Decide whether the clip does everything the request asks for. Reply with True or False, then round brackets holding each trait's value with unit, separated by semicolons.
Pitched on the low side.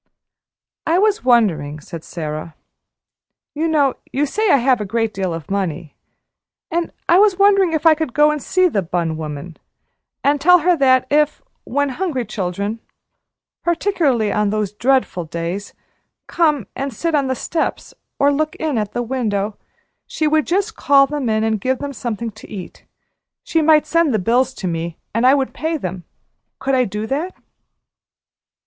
False (260 Hz)